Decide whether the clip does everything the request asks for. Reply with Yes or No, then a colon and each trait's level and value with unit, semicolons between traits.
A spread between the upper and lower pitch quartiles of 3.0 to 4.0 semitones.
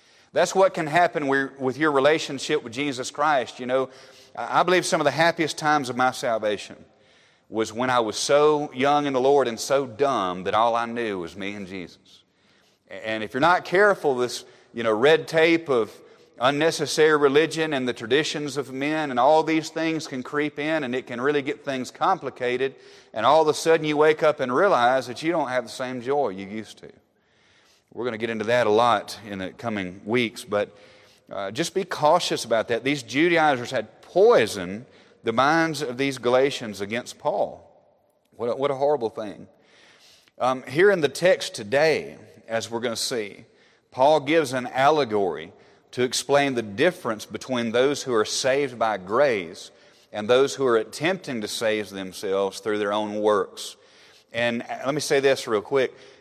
No: average, 4.6 semitones